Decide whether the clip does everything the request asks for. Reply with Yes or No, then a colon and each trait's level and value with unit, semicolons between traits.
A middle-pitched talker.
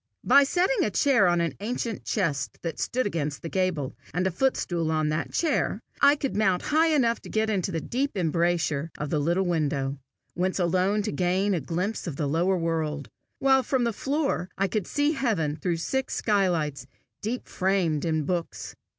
Yes: medium, 180 Hz